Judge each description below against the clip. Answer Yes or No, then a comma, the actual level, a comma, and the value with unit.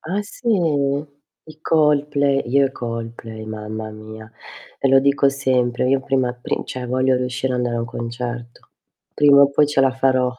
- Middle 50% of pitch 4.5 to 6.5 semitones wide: No, average, 2.8 semitones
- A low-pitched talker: Yes, low, 130 Hz